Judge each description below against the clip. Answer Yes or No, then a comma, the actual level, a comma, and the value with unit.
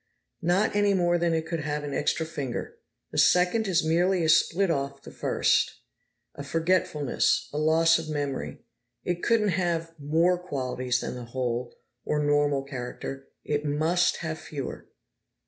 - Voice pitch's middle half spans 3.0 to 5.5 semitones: Yes, average, 3.6 semitones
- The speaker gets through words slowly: No, average, 155 wpm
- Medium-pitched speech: Yes, medium, 160 Hz